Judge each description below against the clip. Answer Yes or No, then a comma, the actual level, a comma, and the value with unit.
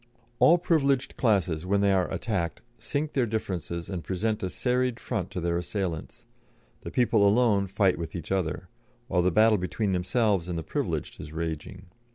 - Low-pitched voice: Yes, very low, 95 Hz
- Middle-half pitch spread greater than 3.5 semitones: Yes, average, 4.5 semitones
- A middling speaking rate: Yes, average, 175 wpm